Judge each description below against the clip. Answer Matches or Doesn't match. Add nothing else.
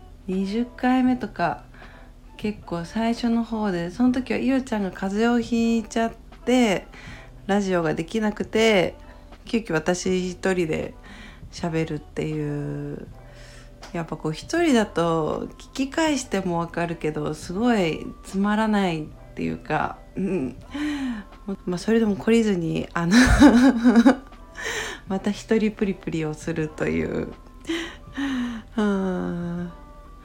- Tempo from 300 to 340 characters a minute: Doesn't match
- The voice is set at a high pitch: Matches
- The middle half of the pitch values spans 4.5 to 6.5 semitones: Matches